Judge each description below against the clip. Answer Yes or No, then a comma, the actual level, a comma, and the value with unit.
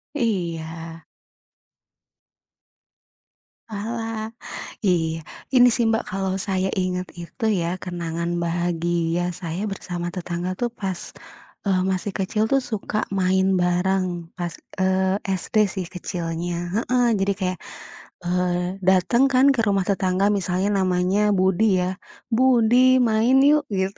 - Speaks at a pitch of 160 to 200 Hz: Yes, high, 190 Hz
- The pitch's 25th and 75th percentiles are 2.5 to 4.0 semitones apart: Yes, average, 3.2 semitones